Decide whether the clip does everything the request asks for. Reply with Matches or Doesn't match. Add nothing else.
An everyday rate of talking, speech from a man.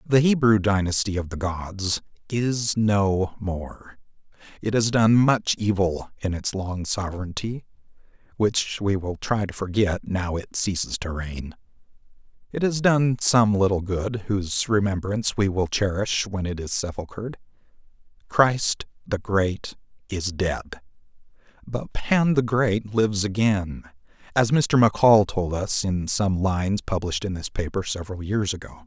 Matches